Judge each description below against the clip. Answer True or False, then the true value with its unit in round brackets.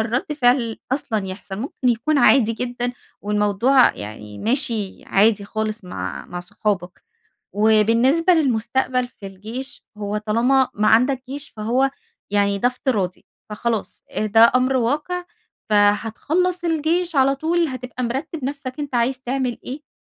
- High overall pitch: True (245 Hz)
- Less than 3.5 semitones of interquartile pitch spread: False (4.2 semitones)